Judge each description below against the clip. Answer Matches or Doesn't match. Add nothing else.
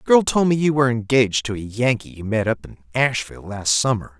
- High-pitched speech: Doesn't match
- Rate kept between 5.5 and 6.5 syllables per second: Matches